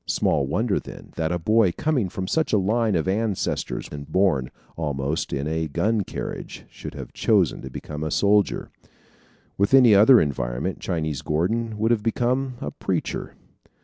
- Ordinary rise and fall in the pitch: No, wide, 6.4 semitones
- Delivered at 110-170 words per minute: Yes, average, 165 wpm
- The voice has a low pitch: Yes, very low, 95 Hz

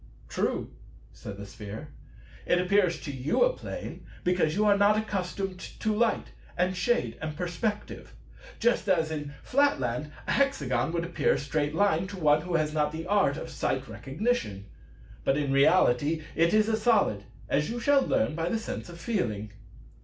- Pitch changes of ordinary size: No, wide, 5.9 semitones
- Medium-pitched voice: Yes, medium, 175 Hz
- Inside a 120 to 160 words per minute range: No, average, 175 wpm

